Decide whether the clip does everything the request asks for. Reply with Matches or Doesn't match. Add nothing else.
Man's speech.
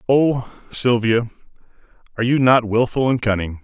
Matches